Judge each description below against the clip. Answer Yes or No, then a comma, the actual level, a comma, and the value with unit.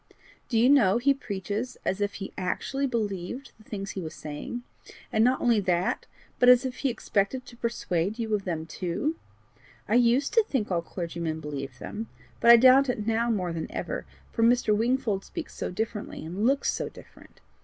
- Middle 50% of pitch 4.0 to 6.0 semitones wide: Yes, average, 5.0 semitones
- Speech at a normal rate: Yes, average, 190 wpm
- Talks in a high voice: Yes, high, 220 Hz